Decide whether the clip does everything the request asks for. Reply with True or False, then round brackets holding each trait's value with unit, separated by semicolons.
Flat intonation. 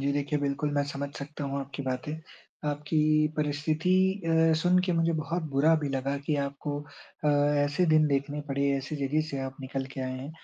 True (1.9 semitones)